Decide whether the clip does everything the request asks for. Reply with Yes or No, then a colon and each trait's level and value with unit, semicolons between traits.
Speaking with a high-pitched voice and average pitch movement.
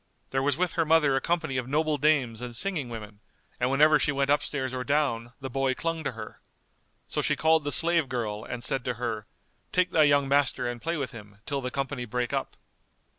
No: low, 135 Hz; average, 3.7 semitones